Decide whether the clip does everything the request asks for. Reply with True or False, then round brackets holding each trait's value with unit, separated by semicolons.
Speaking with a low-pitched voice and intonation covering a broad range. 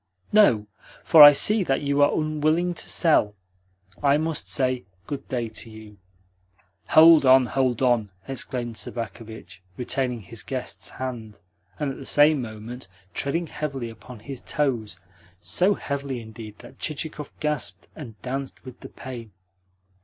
False (130 Hz; 4.3 semitones)